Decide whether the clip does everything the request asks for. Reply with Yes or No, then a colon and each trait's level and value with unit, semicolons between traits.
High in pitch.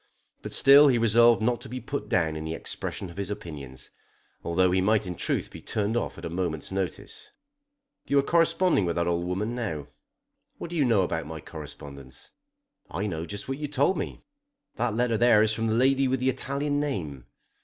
No: low, 105 Hz